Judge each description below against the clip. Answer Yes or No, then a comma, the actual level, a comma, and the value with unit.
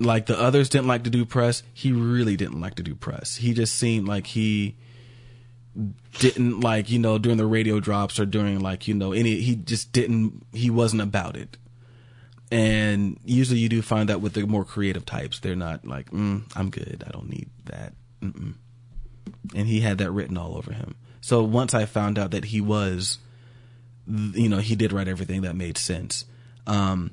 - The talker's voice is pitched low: Yes, low, 115 Hz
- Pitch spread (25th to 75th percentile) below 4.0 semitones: Yes, average, 2.9 semitones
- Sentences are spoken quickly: No, average, 195 wpm